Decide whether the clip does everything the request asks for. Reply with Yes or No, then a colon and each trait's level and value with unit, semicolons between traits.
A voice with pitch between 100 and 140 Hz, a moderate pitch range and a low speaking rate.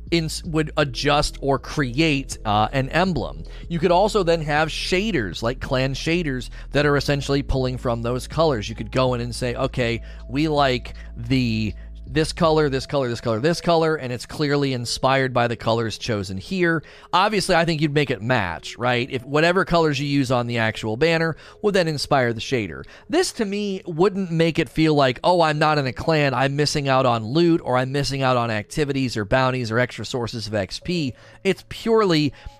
No: low, 135 Hz; average, 4.9 semitones; average, 200 wpm